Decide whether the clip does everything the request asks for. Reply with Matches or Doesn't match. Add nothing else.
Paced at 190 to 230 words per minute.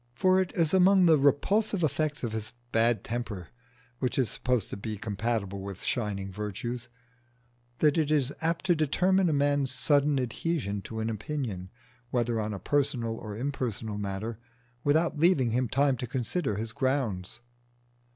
Doesn't match